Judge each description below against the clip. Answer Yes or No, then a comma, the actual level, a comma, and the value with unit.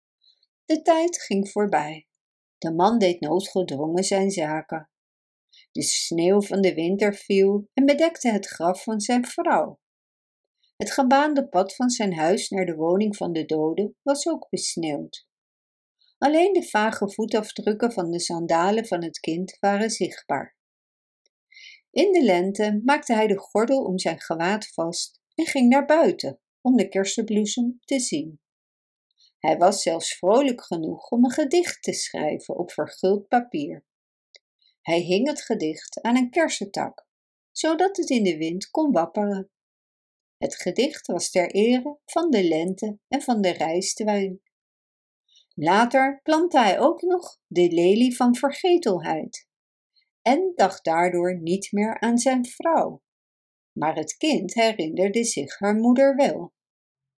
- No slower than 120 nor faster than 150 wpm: Yes, average, 140 wpm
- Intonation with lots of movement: Yes, wide, 7.2 semitones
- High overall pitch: Yes, high, 210 Hz